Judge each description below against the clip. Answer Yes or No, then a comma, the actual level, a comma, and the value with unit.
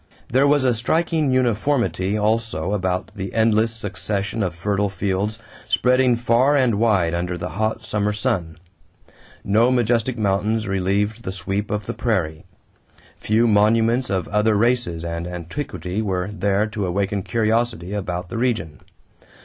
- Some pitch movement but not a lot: Yes, average, 3.6 semitones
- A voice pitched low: Yes, low, 105 Hz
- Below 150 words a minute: Yes, average, 140 wpm